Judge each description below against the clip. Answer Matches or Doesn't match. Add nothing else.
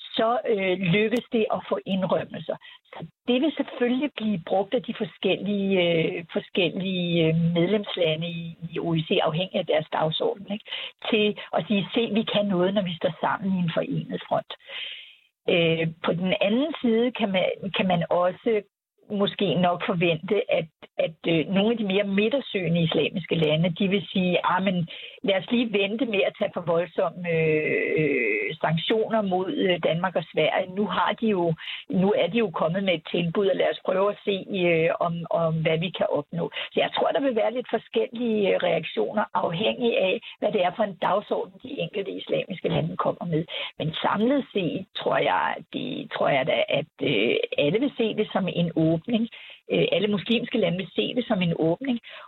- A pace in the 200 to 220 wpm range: Doesn't match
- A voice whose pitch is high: Matches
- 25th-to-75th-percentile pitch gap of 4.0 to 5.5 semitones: Matches